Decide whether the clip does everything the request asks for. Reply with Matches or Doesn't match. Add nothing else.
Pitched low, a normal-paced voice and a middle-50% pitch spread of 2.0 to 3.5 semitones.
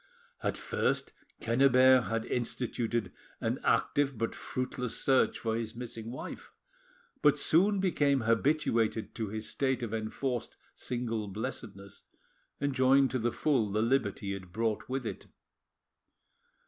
Doesn't match